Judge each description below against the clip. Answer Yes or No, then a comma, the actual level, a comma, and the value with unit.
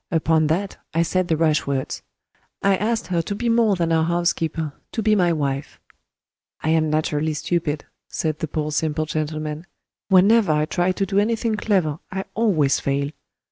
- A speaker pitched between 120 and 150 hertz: No, medium, 165 Hz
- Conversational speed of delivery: Yes, average, 175 wpm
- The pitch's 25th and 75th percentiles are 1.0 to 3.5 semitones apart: No, average, 4.0 semitones